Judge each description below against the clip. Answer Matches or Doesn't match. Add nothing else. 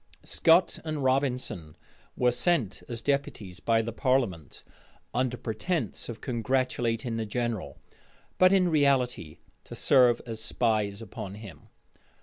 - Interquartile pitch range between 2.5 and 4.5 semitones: Matches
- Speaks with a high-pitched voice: Doesn't match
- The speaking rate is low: Matches